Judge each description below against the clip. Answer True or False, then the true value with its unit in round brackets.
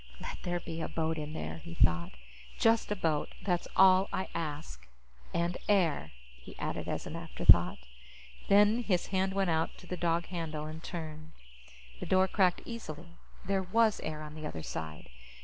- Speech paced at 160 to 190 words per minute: True (175 wpm)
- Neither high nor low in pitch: True (170 Hz)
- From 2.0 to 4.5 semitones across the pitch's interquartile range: True (3.5 semitones)